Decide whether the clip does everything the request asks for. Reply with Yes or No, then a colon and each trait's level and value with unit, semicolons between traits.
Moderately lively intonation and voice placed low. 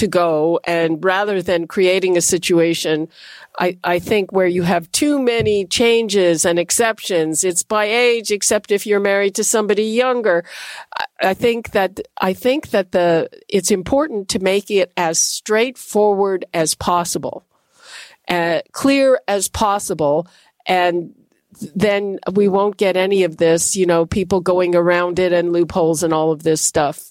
No: average, 3.3 semitones; high, 190 Hz